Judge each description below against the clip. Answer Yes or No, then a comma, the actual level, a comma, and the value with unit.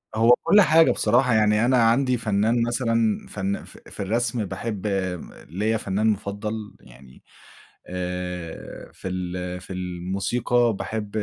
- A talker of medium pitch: No, low, 105 Hz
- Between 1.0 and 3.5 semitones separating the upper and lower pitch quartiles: No, average, 3.9 semitones